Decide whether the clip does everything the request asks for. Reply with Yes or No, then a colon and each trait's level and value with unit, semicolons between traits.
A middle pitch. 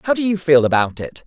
Yes: medium, 160 Hz